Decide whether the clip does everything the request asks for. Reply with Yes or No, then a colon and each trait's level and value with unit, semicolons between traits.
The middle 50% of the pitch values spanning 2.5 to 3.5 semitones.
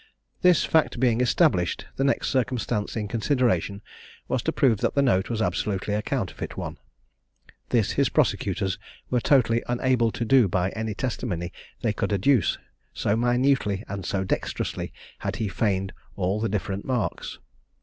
No: average, 4.3 semitones